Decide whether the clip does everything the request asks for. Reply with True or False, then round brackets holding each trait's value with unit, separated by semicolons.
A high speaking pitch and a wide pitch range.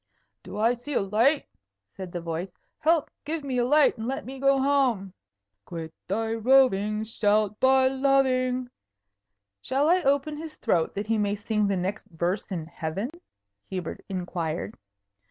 True (220 Hz; 6.1 semitones)